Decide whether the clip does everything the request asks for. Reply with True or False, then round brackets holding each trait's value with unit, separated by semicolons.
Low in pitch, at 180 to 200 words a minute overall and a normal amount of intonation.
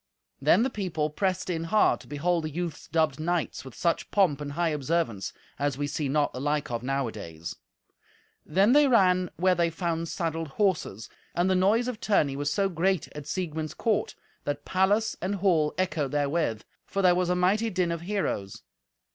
False (170 Hz; 185 wpm; 4.2 semitones)